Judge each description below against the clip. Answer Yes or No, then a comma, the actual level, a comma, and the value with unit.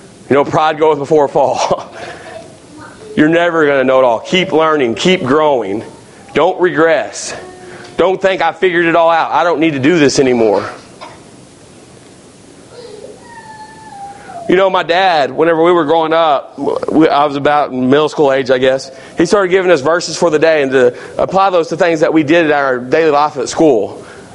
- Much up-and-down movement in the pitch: No, average, 3.8 semitones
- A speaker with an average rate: Yes, average, 180 wpm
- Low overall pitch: No, medium, 165 Hz